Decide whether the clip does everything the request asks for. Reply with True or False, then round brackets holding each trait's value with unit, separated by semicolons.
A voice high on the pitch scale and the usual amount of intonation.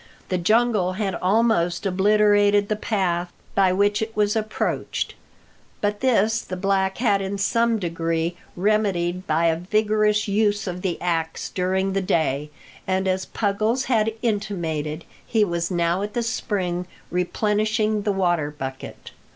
True (195 Hz; 3.3 semitones)